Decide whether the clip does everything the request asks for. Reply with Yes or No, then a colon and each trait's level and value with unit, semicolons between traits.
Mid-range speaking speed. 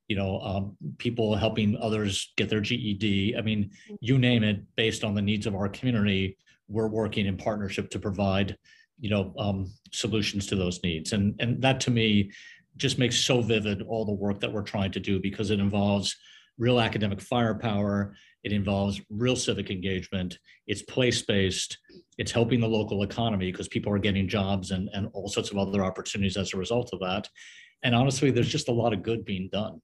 Yes: average, 195 wpm